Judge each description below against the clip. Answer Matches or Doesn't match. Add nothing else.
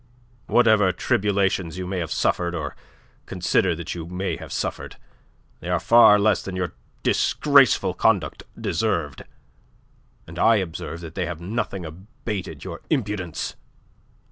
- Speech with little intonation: Doesn't match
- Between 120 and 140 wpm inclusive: Matches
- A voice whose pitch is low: Matches